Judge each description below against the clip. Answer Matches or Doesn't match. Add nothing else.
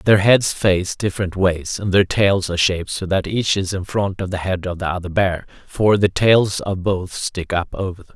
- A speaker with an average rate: Doesn't match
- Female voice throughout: Doesn't match